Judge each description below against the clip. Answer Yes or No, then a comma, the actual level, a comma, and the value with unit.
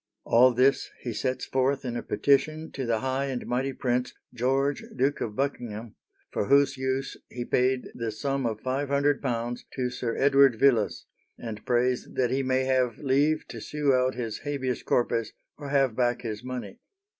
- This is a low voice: Yes, low, 130 Hz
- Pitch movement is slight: Yes, narrow, 2.2 semitones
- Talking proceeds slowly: No, average, 170 wpm